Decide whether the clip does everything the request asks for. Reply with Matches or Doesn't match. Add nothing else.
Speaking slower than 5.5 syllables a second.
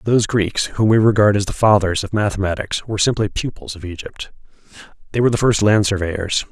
Doesn't match